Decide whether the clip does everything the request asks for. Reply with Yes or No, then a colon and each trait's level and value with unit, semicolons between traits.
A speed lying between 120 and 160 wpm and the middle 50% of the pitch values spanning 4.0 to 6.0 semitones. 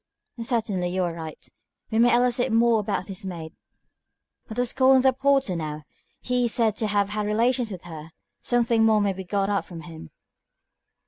No: average, 190 wpm; average, 5.1 semitones